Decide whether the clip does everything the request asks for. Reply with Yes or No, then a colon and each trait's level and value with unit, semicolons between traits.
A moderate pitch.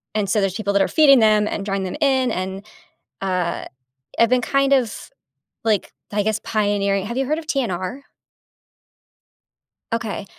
No: high, 215 Hz